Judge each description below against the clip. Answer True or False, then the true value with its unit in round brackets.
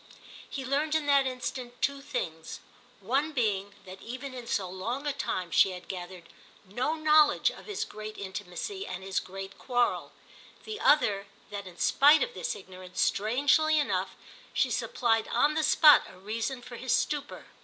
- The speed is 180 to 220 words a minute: False (165 wpm)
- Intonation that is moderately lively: False (6.9 semitones)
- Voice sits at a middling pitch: False (245 Hz)